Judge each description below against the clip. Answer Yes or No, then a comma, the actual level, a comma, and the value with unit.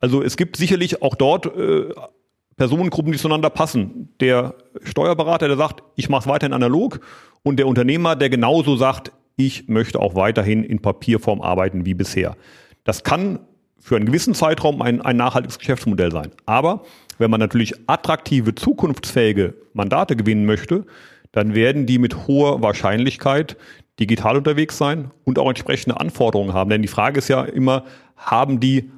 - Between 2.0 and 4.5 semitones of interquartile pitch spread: No, average, 5.2 semitones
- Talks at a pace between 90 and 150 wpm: No, average, 160 wpm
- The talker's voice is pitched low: Yes, low, 130 Hz